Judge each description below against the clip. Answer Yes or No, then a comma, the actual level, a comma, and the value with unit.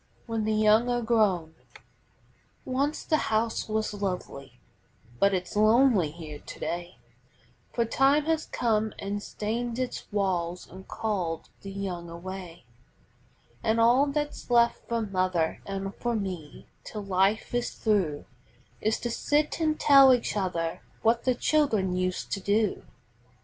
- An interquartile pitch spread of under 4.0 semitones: No, average, 4.4 semitones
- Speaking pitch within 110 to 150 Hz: No, high, 210 Hz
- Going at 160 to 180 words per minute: No, average, 140 wpm